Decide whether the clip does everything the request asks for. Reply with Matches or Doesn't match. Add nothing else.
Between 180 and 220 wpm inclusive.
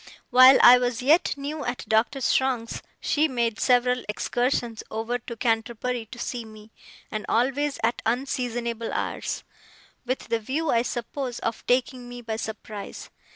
Doesn't match